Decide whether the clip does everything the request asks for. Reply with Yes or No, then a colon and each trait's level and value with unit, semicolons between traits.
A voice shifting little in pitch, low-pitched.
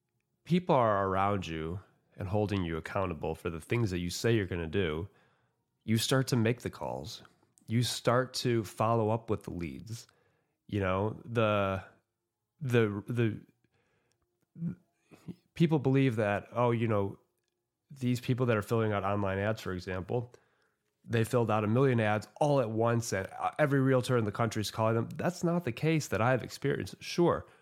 No: average, 3.9 semitones; low, 115 Hz